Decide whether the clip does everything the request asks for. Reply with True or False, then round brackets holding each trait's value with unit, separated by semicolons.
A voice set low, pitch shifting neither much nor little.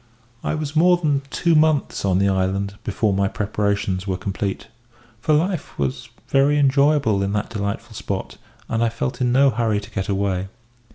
False (110 Hz; 6.4 semitones)